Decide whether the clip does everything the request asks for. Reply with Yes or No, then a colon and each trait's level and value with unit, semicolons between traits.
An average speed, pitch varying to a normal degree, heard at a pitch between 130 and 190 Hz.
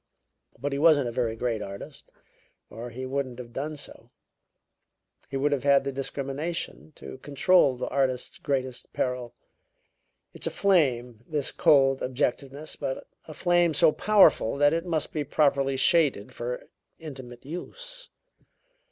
Yes: average, 145 wpm; average, 3.4 semitones; medium, 140 Hz